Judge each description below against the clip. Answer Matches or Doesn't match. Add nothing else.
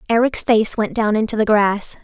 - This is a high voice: Matches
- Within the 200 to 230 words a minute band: Matches